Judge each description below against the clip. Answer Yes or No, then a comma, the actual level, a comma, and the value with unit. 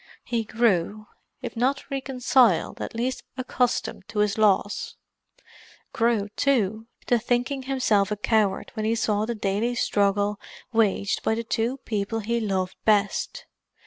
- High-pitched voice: Yes, high, 220 Hz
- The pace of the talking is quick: No, average, 140 wpm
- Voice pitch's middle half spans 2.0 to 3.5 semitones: Yes, average, 2.9 semitones